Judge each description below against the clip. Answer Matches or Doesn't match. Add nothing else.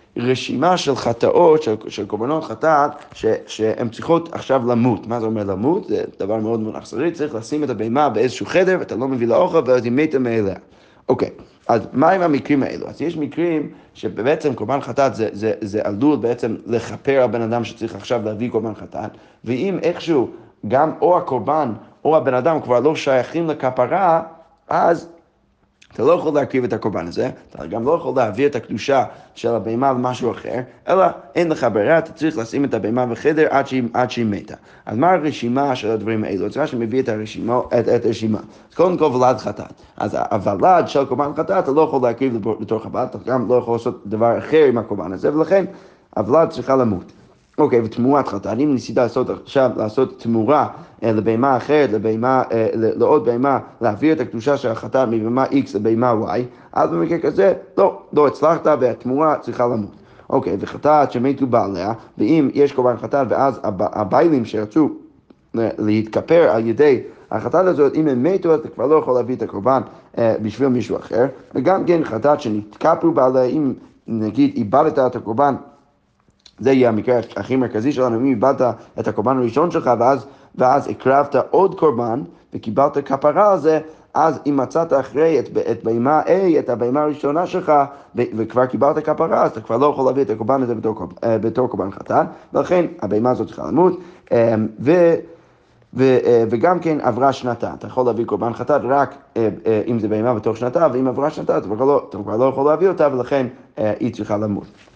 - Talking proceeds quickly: Matches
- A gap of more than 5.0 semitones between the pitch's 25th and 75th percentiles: Doesn't match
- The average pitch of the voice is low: Matches